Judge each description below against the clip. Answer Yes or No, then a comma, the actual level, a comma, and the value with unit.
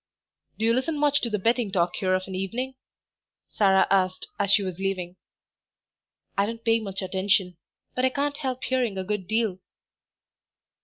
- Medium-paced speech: Yes, average, 170 wpm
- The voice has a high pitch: Yes, high, 205 Hz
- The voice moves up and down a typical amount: Yes, average, 4.4 semitones